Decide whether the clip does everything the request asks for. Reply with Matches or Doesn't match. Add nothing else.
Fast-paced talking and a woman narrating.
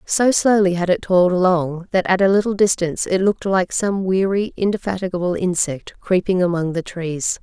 Doesn't match